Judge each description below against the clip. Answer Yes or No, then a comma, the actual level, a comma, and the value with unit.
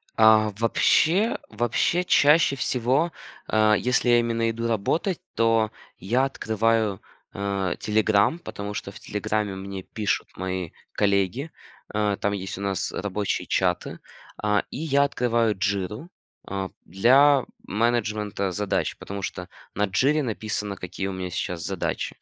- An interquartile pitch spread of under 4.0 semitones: Yes, average, 3.5 semitones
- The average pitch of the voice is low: Yes, low, 110 Hz